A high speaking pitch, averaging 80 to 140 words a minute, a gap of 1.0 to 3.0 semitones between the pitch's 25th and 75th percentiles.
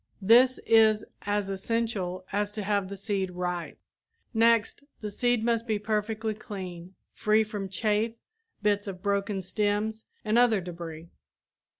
Yes: high, 210 Hz; slow, 135 wpm; narrow, 2.5 semitones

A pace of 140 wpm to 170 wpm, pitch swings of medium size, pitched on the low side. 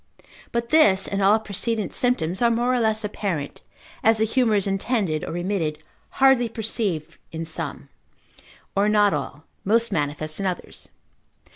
No: average, 150 wpm; average, 4.7 semitones; high, 205 Hz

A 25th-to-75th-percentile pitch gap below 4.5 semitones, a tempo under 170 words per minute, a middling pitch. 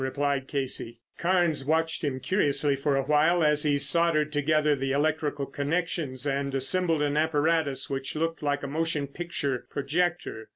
Yes: average, 2.7 semitones; average, 155 wpm; medium, 145 Hz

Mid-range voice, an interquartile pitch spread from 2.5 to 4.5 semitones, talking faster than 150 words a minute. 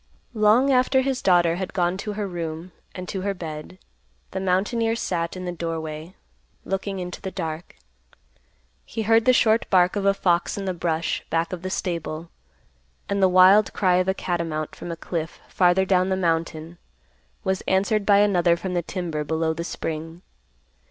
Yes: medium, 180 Hz; average, 2.8 semitones; average, 180 wpm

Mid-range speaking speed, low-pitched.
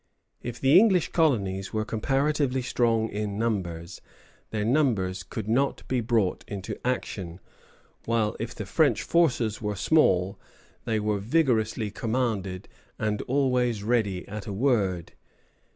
No: slow, 130 wpm; low, 110 Hz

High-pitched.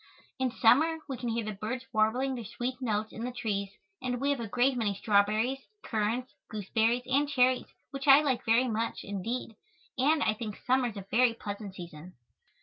Yes: high, 235 Hz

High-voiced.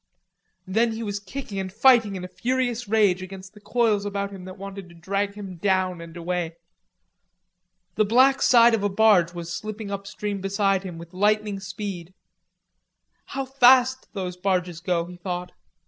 Yes: high, 195 Hz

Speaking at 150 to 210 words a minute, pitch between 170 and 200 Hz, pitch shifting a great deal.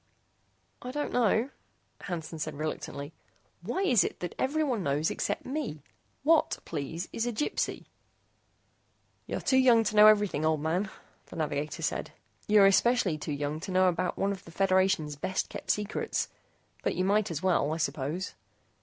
Yes: average, 165 wpm; medium, 185 Hz; wide, 5.8 semitones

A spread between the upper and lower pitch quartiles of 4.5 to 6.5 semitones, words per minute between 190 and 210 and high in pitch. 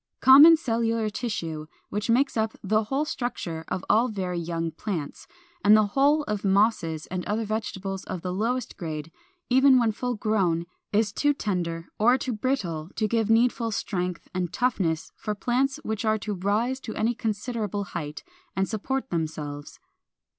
No: average, 4.8 semitones; average, 165 wpm; high, 210 Hz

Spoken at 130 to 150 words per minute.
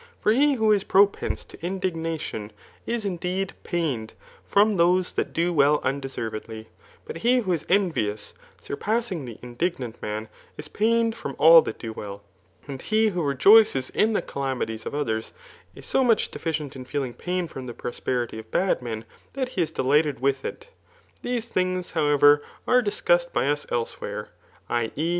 No: average, 170 wpm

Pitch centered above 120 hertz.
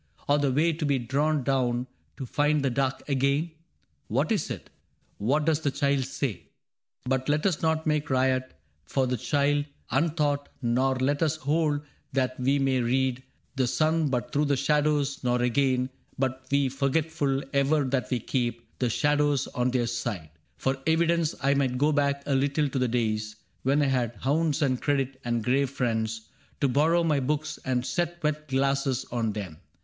Yes: low, 135 Hz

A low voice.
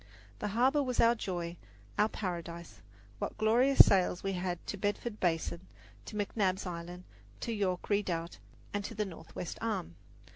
No: high, 195 Hz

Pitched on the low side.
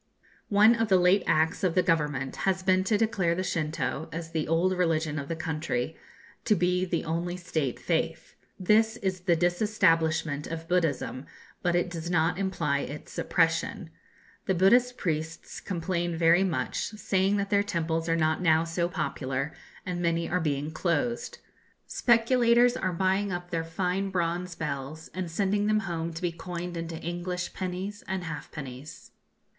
No: medium, 175 Hz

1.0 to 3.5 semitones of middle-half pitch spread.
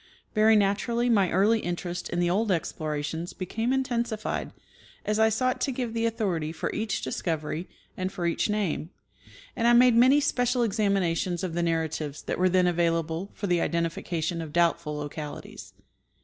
No: average, 5.0 semitones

